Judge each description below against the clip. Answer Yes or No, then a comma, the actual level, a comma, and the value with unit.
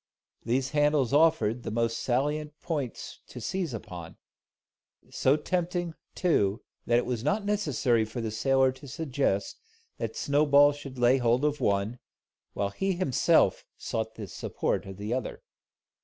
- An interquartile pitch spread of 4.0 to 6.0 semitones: Yes, average, 4.6 semitones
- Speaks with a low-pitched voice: Yes, low, 130 Hz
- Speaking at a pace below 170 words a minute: Yes, average, 145 wpm